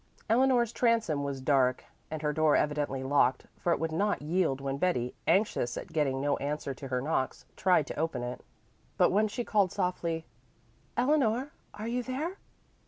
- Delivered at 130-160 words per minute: No, average, 170 wpm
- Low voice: No, medium, 160 Hz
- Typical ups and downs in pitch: No, wide, 7.5 semitones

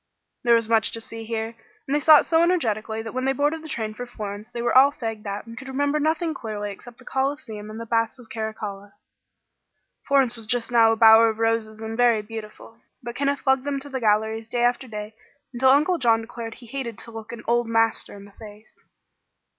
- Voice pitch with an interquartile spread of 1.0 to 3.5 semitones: Yes, average, 3.0 semitones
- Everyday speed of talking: No, fast, 225 wpm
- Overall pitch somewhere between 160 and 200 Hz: No, high, 230 Hz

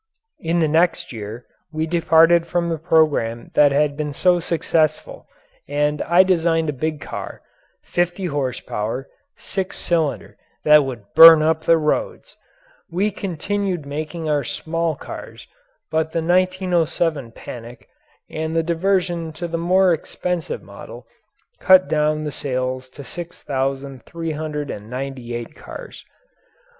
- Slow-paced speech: Yes, slow, 125 wpm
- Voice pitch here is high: No, medium, 160 Hz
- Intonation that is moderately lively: Yes, average, 3.2 semitones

